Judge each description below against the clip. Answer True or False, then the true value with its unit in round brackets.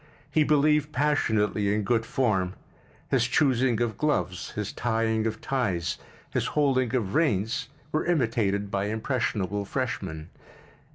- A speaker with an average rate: False (120 wpm)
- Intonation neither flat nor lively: True (4.7 semitones)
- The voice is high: False (115 Hz)